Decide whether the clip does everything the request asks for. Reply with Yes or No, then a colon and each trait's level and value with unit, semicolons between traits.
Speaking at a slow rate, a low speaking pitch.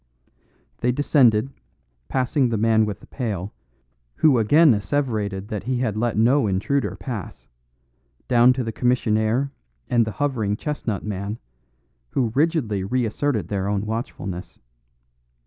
Yes: slow, 130 wpm; low, 115 Hz